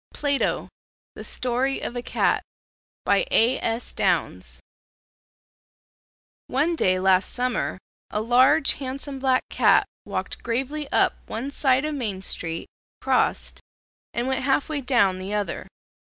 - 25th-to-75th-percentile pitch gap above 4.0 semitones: No, average, 3.6 semitones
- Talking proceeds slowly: Yes, slow, 130 wpm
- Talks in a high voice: Yes, very high, 255 Hz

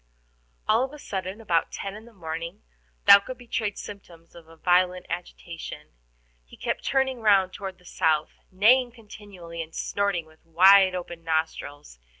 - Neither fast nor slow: Yes, average, 150 wpm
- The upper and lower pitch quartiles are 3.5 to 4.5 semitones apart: Yes, average, 3.9 semitones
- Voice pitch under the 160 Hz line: No, medium, 185 Hz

